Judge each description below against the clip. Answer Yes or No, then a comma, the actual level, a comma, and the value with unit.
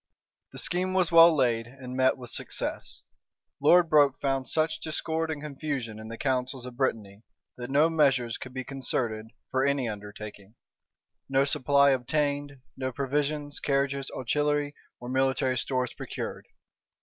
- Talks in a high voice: No, low, 135 Hz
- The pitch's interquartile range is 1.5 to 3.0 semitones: Yes, average, 2.7 semitones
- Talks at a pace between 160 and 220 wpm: No, average, 145 wpm